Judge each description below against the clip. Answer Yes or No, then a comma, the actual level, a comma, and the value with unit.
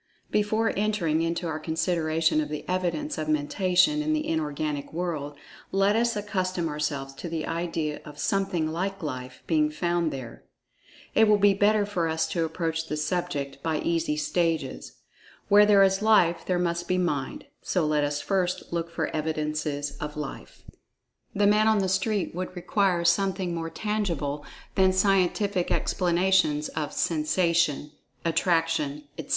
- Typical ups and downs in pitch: Yes, average, 3.9 semitones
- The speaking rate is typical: Yes, average, 150 wpm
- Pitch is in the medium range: Yes, medium, 170 Hz